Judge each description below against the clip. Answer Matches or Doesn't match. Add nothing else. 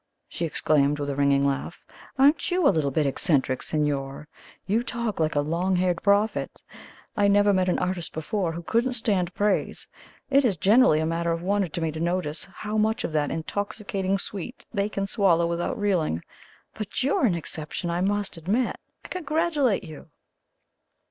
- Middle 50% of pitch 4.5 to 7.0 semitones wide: Matches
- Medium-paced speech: Matches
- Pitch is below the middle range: Doesn't match